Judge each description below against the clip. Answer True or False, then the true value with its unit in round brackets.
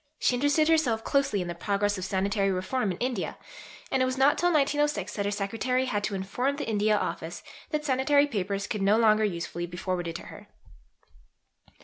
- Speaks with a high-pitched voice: True (215 Hz)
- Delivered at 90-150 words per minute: False (195 wpm)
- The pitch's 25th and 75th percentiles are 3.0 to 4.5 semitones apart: False (5.4 semitones)